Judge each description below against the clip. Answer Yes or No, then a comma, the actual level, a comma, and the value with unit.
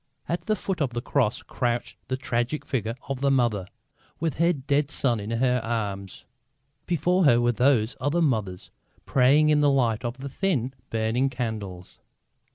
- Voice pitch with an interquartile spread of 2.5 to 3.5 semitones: No, average, 4.0 semitones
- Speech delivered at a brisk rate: No, average, 165 wpm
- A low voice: Yes, low, 125 Hz